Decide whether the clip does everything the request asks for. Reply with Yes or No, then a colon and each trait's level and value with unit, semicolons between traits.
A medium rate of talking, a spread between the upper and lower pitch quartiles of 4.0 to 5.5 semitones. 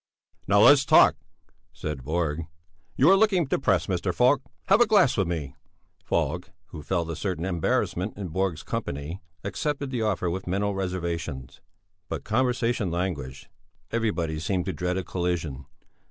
Yes: average, 150 wpm; average, 5.1 semitones